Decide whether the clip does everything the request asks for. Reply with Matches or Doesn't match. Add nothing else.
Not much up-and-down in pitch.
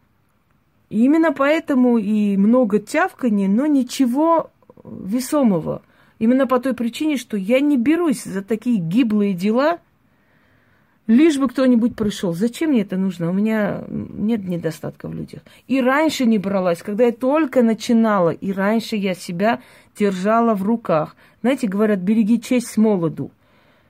Doesn't match